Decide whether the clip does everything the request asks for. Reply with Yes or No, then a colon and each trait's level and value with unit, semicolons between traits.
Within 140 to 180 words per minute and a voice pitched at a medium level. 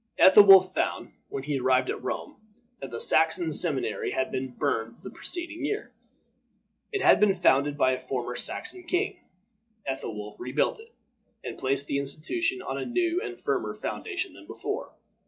Yes: average, 160 wpm; medium, 155 Hz